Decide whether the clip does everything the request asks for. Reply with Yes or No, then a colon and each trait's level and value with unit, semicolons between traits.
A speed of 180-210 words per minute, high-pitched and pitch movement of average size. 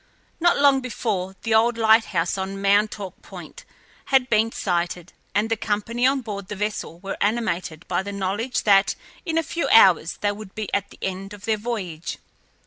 Yes: average, 185 wpm; high, 205 Hz; average, 3.0 semitones